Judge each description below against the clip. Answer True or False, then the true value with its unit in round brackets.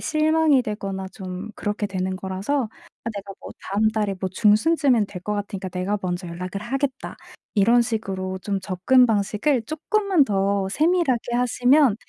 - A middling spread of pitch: True (4.9 semitones)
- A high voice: True (210 Hz)